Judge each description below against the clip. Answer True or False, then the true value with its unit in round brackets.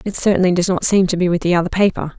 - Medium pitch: True (180 Hz)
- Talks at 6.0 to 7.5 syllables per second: True (7.2 syllables/s)